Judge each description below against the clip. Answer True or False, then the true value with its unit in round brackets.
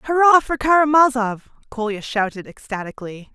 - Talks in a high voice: True (250 Hz)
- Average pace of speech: False (110 wpm)